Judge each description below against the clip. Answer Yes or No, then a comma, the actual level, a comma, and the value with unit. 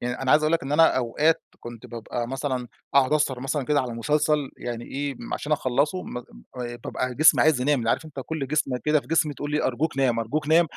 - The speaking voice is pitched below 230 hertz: Yes, medium, 140 Hz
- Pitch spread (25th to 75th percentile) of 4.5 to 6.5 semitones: No, average, 3.5 semitones